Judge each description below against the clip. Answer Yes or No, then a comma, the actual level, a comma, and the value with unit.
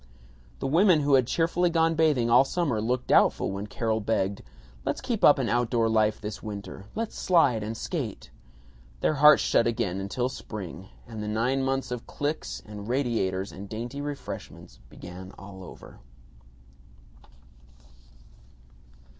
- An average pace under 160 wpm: Yes, average, 145 wpm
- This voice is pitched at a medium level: No, low, 120 Hz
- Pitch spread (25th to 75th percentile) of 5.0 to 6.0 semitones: Yes, wide, 5.4 semitones